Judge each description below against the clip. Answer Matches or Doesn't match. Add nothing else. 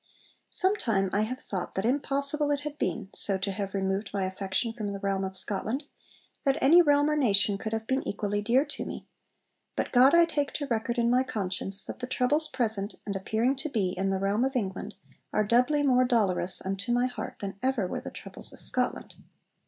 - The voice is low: Doesn't match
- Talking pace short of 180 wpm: Doesn't match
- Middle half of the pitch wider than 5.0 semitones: Matches